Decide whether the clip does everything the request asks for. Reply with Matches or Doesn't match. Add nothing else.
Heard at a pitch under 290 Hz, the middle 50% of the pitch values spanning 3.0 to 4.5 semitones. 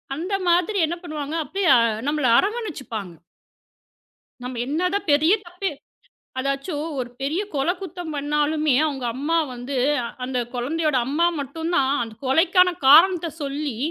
Doesn't match